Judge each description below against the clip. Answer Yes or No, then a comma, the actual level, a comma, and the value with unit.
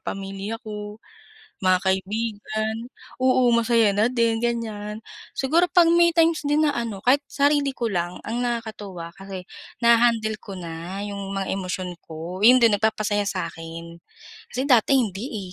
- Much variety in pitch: No, average, 3.8 semitones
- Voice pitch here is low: No, high, 215 Hz